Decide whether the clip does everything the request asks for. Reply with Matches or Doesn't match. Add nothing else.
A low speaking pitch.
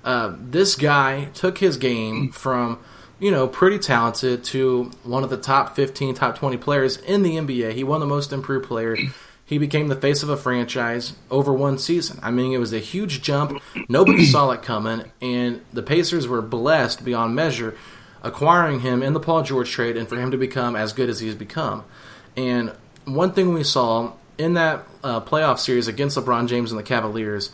Matches